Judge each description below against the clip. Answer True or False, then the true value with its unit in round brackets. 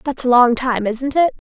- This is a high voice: True (255 Hz)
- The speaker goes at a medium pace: False (240 wpm)